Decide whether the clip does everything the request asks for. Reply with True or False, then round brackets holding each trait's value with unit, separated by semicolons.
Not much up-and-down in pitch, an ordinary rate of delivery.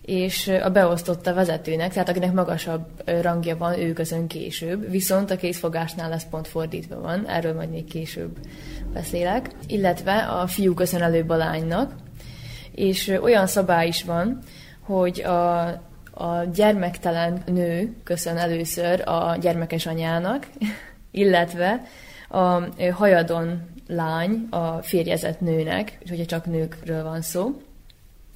True (2.0 semitones; 125 wpm)